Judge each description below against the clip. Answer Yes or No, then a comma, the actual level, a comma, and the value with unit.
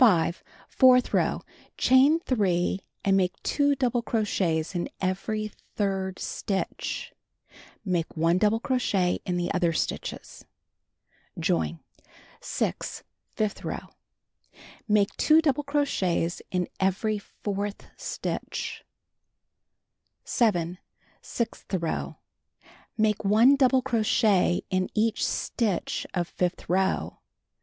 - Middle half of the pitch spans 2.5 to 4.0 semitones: No, average, 4.7 semitones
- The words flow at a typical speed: No, slow, 90 wpm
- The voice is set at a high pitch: Yes, high, 205 Hz